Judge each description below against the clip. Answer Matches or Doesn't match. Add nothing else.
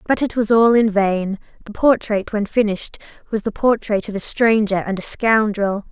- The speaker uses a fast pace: Doesn't match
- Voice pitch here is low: Doesn't match